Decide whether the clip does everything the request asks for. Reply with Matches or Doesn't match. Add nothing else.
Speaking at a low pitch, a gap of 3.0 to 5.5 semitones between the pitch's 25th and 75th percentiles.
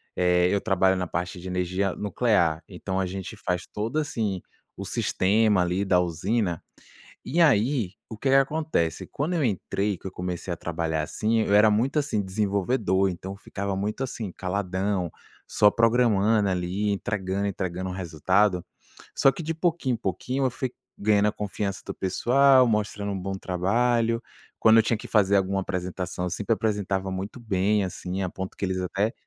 Matches